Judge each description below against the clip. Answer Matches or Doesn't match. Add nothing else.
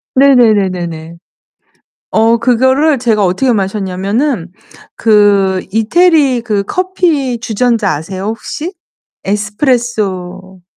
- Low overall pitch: Doesn't match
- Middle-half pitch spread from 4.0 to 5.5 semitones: Matches